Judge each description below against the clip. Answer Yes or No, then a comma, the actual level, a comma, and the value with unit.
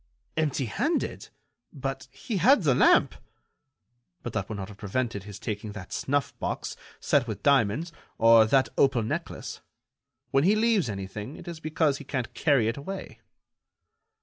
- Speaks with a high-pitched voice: No, low, 130 Hz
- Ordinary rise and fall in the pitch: No, wide, 6.4 semitones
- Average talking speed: Yes, average, 155 wpm